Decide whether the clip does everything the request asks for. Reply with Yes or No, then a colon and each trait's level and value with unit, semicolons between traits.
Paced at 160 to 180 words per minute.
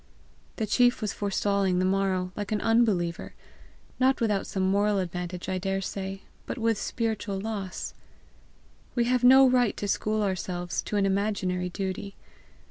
No: average, 150 wpm